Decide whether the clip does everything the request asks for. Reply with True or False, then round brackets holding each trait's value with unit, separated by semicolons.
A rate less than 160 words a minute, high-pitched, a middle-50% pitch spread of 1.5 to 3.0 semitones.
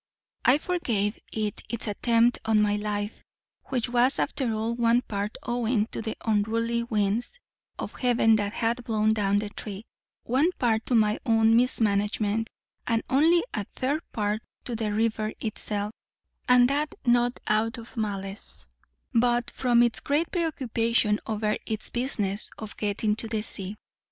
True (150 wpm; 225 Hz; 2.4 semitones)